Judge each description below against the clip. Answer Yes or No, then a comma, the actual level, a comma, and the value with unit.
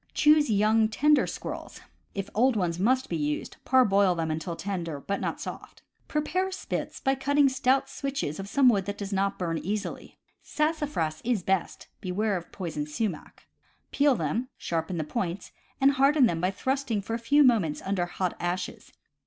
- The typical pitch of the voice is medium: No, high, 205 Hz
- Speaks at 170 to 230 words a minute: Yes, average, 180 wpm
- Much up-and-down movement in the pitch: Yes, wide, 7.1 semitones